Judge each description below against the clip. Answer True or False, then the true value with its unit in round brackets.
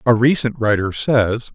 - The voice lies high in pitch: False (115 Hz)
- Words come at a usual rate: True (155 wpm)